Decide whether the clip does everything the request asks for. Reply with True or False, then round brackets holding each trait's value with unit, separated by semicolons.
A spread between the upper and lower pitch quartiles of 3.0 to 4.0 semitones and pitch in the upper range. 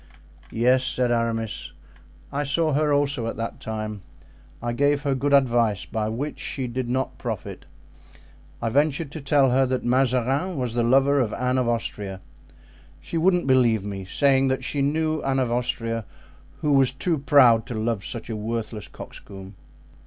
False (3.5 semitones; 130 Hz)